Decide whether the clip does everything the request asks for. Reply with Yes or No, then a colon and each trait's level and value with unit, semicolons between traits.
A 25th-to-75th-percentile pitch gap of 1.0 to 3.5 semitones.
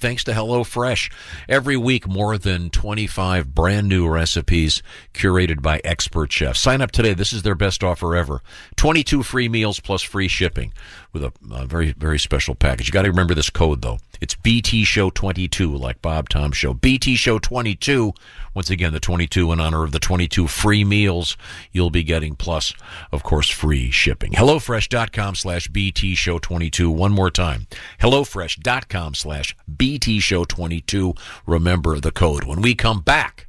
No: average, 4.5 semitones